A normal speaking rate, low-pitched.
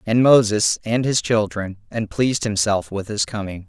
Yes: average, 180 wpm; low, 105 Hz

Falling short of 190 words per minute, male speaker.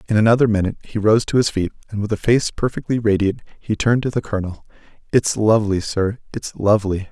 No: average, 200 wpm; male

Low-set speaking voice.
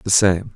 Yes: very low, 95 Hz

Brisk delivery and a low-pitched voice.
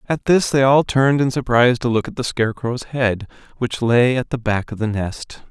Yes: fast, 230 wpm; low, 125 Hz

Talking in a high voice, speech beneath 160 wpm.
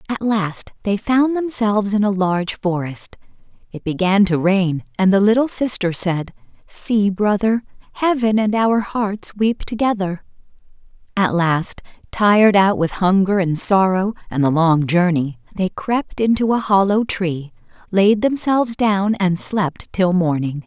Yes: high, 195 Hz; average, 150 wpm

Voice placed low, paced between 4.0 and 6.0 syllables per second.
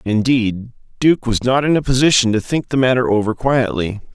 Yes: low, 120 Hz; 5.2 syllables/s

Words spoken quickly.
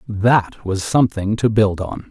No: average, 170 wpm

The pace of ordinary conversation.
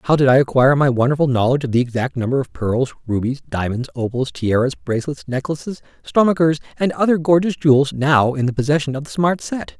Yes: average, 195 wpm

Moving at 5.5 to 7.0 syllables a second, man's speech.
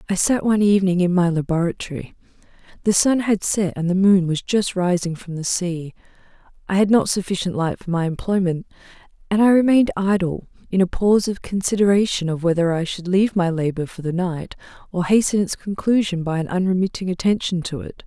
No: 5.8 syllables/s; female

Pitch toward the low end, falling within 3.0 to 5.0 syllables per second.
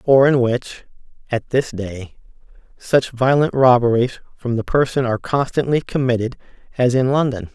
Yes: low, 125 Hz; 4.7 syllables/s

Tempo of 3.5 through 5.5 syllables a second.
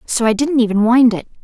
No: 5.8 syllables/s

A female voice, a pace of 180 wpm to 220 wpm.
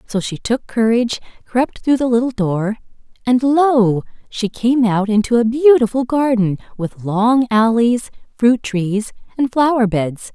No: female; average, 150 wpm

